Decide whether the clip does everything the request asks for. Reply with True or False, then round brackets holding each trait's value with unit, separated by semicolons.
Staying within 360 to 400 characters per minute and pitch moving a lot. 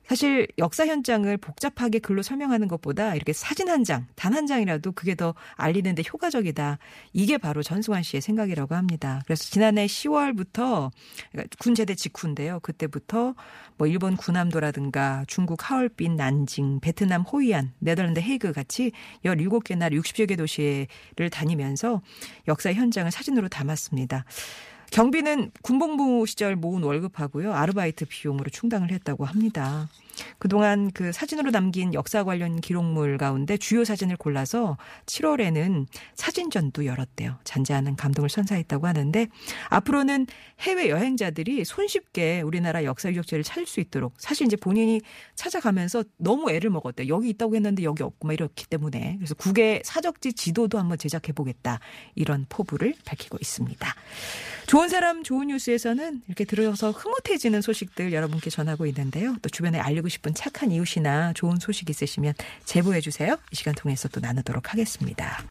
True (375 characters per minute; 6.7 semitones)